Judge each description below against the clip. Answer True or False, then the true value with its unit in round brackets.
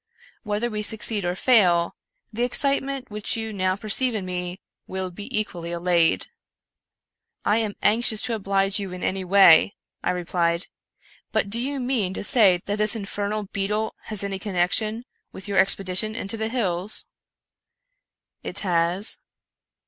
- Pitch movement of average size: True (3.1 semitones)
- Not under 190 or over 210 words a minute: False (160 wpm)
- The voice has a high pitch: True (200 Hz)